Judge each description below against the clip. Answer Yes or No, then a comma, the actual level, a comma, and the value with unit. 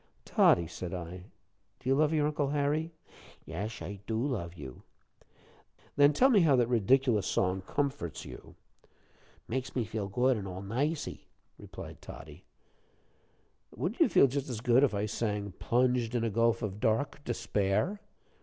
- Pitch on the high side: No, low, 115 Hz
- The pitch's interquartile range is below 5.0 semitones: No, wide, 5.6 semitones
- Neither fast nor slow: Yes, average, 155 wpm